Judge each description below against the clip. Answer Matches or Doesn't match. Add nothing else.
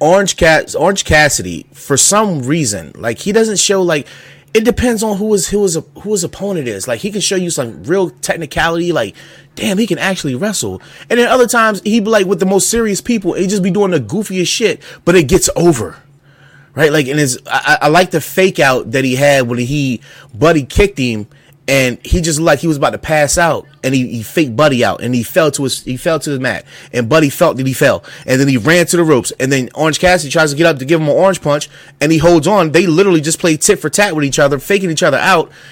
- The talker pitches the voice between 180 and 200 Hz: Doesn't match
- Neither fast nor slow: Doesn't match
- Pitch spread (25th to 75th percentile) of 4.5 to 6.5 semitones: Matches